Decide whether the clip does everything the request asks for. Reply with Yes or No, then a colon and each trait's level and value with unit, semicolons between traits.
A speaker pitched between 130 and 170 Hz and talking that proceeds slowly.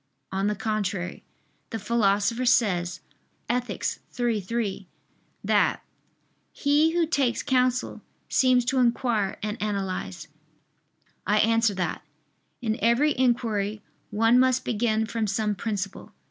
No: high, 225 Hz; slow, 115 wpm